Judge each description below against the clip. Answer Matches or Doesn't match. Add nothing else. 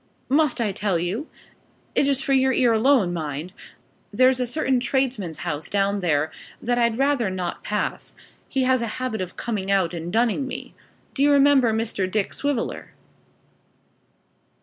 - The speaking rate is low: Doesn't match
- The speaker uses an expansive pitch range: Matches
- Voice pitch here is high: Matches